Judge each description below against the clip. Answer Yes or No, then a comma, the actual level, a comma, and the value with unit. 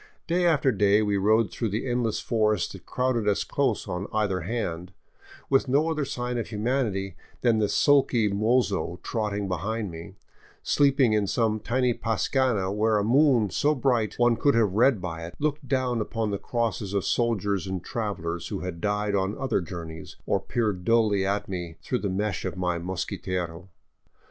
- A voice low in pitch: Yes, low, 105 Hz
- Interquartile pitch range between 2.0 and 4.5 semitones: Yes, average, 4.1 semitones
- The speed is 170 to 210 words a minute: Yes, average, 180 wpm